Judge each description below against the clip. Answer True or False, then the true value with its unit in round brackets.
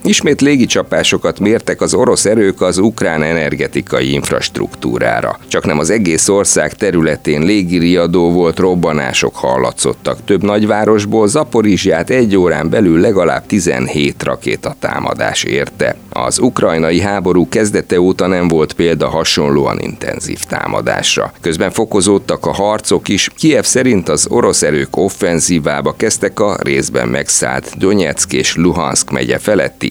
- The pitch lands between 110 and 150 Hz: False (95 Hz)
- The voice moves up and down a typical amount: True (3.7 semitones)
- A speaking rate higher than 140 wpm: False (125 wpm)